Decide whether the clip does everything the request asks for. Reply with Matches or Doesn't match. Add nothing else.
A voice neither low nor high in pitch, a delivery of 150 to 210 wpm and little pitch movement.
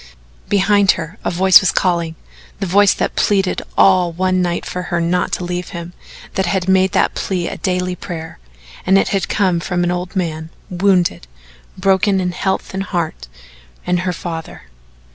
Matches